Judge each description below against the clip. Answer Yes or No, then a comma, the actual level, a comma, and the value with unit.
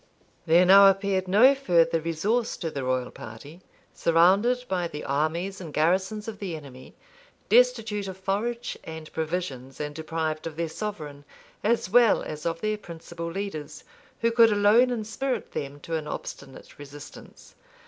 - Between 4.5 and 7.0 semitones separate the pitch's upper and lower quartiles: Yes, average, 5.2 semitones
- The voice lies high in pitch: No, medium, 175 Hz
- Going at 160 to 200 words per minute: No, average, 150 wpm